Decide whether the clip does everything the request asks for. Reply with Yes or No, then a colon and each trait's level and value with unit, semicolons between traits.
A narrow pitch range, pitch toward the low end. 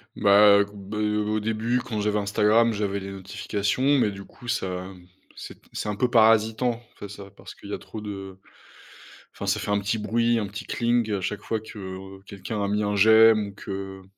Yes: narrow, 1.9 semitones; low, 105 Hz